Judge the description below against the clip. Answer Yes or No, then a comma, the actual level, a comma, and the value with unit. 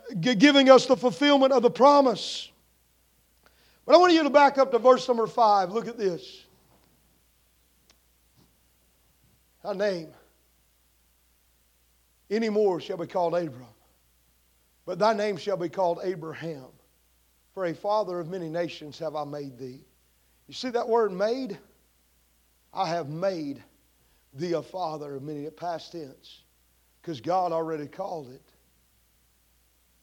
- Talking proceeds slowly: Yes, slow, 130 wpm